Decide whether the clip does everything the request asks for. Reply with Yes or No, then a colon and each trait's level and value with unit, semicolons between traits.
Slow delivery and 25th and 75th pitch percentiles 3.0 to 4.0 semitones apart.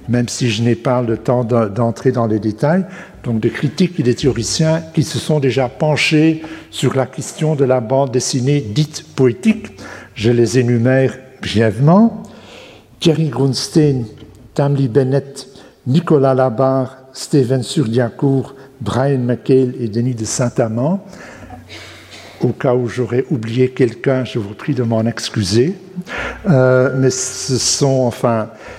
Yes: slow, 140 wpm; average, 3.3 semitones